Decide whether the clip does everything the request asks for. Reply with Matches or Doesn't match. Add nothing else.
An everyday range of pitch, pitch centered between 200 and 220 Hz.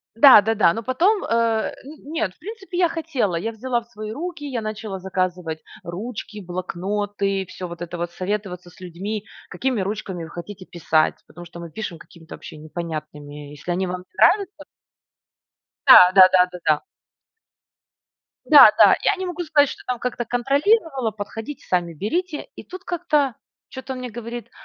Doesn't match